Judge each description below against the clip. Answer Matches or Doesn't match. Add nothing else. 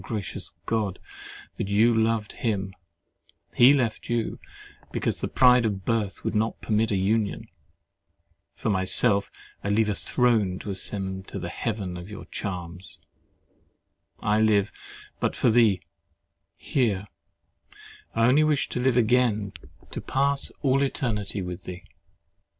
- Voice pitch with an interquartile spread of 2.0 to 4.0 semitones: Matches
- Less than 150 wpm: Matches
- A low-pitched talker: Matches